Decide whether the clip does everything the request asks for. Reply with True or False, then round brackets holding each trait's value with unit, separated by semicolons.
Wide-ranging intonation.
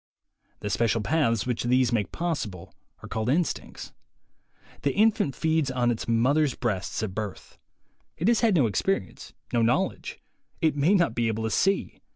True (6.1 semitones)